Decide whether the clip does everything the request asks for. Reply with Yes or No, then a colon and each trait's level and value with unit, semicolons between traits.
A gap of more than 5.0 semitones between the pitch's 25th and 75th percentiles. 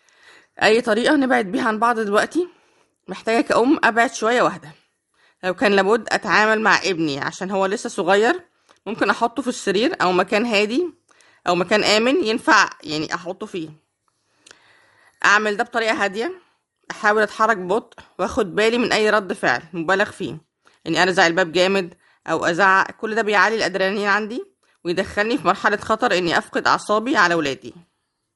No: average, 3.7 semitones